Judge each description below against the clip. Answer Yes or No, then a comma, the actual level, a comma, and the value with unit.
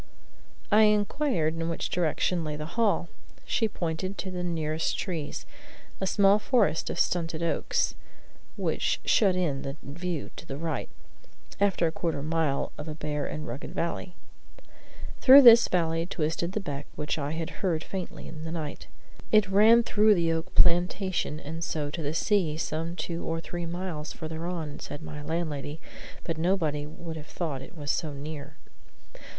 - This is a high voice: No, medium, 165 Hz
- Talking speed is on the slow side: No, average, 170 wpm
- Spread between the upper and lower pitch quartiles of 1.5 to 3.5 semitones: Yes, average, 3.1 semitones